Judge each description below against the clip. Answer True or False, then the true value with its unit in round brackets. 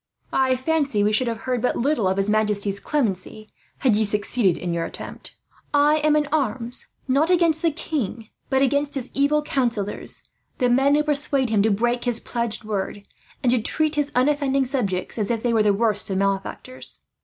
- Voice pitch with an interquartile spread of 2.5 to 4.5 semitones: False (5.1 semitones)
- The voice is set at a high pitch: True (245 Hz)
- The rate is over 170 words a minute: True (190 wpm)